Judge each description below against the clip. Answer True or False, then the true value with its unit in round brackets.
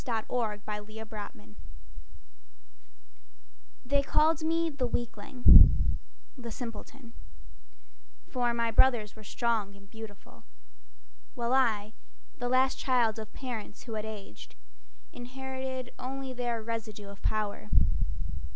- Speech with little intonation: False (3.2 semitones)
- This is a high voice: True (235 Hz)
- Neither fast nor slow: False (105 wpm)